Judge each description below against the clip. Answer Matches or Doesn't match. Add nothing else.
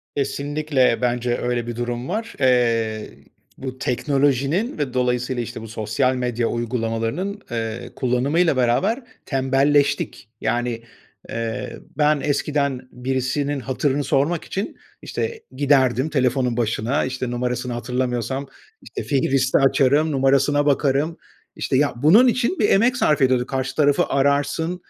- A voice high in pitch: Doesn't match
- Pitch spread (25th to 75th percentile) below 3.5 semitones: Matches